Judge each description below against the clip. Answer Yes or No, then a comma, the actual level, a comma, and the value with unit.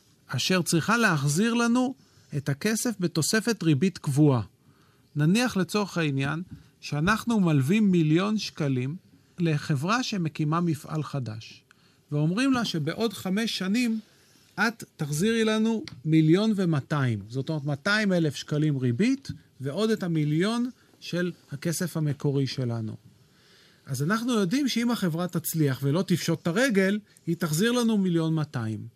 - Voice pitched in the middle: Yes, medium, 170 Hz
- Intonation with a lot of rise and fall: Yes, wide, 6.4 semitones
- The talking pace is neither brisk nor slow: Yes, average, 120 wpm